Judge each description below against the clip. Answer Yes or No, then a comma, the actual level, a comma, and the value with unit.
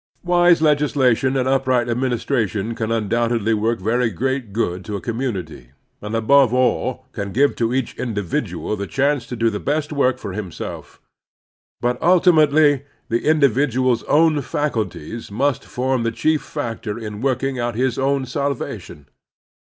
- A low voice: Yes, low, 125 Hz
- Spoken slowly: No, average, 155 wpm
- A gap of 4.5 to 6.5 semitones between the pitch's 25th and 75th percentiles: No, average, 3.8 semitones